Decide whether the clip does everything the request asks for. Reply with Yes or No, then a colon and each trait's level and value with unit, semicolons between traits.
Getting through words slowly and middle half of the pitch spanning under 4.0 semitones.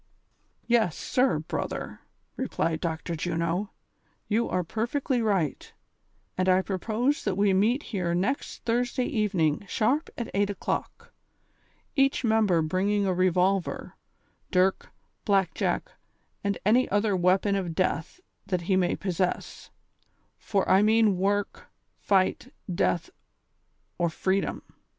Yes: slow, 125 wpm; average, 3.4 semitones